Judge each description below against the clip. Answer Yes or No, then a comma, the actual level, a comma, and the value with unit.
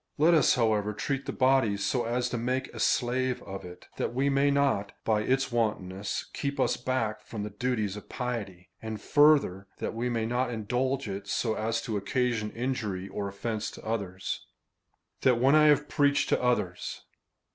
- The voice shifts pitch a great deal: No, average, 3.9 semitones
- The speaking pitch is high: No, low, 115 Hz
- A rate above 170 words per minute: Yes, average, 180 wpm